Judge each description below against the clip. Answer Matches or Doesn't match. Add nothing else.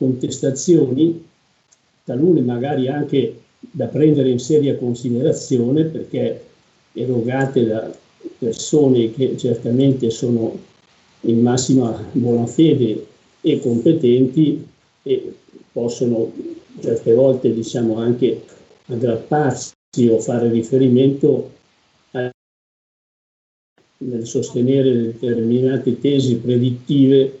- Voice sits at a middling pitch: Doesn't match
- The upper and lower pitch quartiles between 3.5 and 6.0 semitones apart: Doesn't match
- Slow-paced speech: Matches